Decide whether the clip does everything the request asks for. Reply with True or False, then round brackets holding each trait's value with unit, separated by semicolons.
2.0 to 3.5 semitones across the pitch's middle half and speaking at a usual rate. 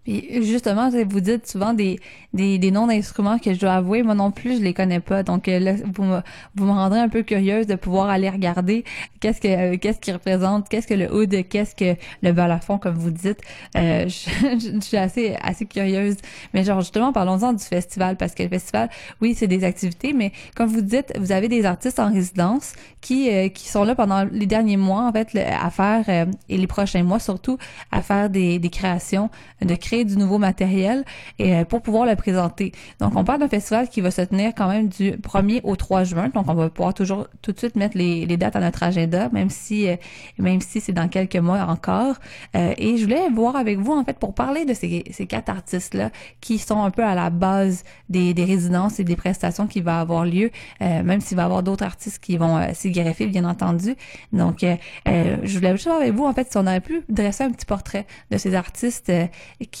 False (3.2 semitones; 230 wpm)